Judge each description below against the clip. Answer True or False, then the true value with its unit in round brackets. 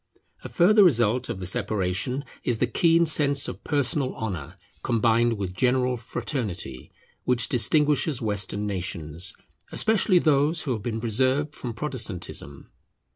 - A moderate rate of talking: False (130 wpm)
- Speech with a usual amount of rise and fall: False (5.8 semitones)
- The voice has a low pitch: True (120 Hz)